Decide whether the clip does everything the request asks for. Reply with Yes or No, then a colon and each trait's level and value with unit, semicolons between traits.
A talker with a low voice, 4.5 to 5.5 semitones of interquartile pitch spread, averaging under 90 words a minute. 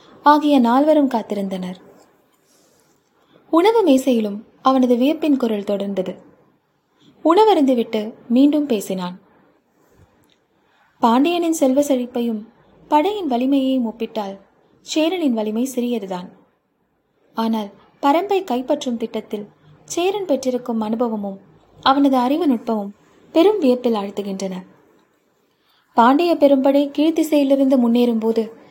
No: high, 245 Hz; average, 4.9 semitones; average, 80 wpm